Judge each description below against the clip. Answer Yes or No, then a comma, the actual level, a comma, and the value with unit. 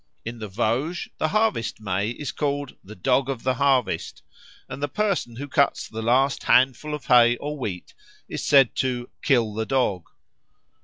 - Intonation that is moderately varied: Yes, average, 3.8 semitones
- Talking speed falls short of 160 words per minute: No, average, 170 wpm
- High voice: No, low, 130 Hz